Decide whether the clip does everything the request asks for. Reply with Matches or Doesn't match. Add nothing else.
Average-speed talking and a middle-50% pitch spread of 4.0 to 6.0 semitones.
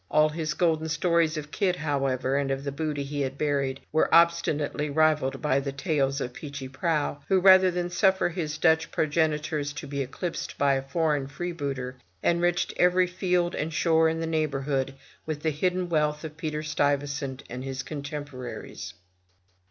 Doesn't match